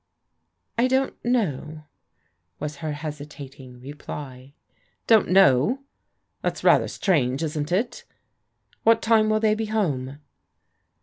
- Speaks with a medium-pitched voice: Yes, medium, 155 Hz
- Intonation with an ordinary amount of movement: No, wide, 7.5 semitones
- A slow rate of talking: Yes, slow, 120 wpm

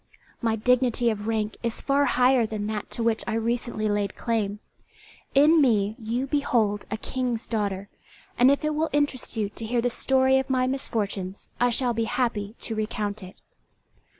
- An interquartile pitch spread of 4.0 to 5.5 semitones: No, average, 3.2 semitones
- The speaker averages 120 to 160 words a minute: No, average, 180 wpm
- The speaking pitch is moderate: No, high, 230 Hz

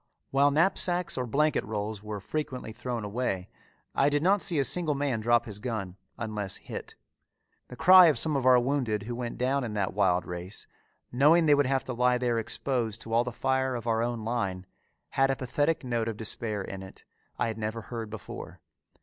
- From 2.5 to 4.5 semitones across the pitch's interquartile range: Yes, average, 4.2 semitones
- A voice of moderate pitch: No, low, 120 Hz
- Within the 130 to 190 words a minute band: No, average, 200 wpm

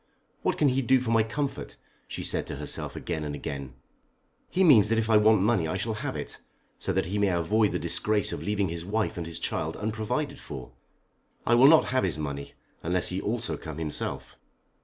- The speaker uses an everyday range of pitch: No, wide, 5.8 semitones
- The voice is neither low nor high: No, low, 105 Hz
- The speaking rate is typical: No, fast, 210 wpm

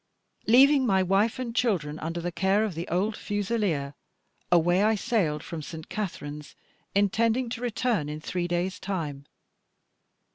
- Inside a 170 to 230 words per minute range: No, average, 145 wpm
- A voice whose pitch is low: No, high, 190 Hz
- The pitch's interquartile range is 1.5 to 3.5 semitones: No, average, 5.1 semitones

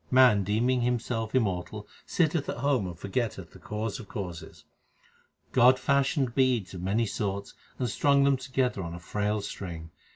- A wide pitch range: No, average, 4.7 semitones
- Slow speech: No, average, 170 wpm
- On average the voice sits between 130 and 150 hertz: No, low, 115 Hz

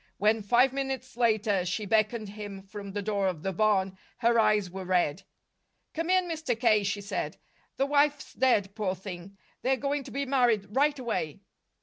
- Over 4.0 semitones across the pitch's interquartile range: Yes, average, 4.9 semitones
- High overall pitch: Yes, high, 215 Hz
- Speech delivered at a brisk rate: No, average, 180 wpm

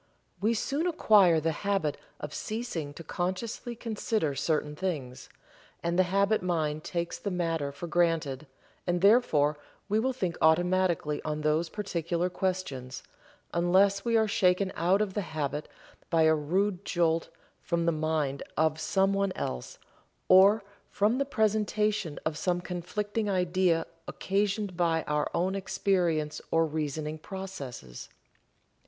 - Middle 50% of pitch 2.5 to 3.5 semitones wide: No, average, 4.1 semitones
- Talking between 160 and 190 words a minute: No, slow, 135 wpm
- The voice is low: No, medium, 175 Hz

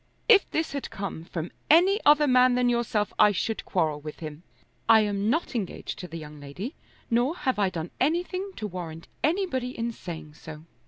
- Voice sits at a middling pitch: No, high, 220 Hz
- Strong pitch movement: Yes, wide, 9.0 semitones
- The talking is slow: No, average, 190 wpm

